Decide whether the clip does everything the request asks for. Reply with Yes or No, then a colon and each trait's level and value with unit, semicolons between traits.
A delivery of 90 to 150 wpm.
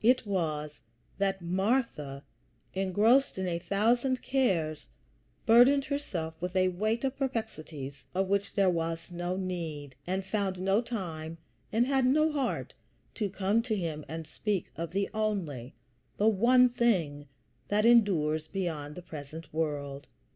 Yes: average, 140 wpm